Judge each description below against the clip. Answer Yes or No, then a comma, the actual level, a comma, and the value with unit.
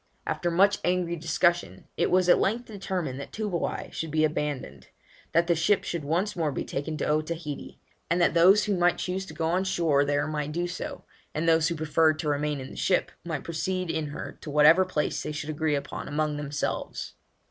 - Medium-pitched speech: Yes, medium, 160 Hz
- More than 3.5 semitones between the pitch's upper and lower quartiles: No, average, 3.0 semitones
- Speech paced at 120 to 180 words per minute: No, fast, 205 wpm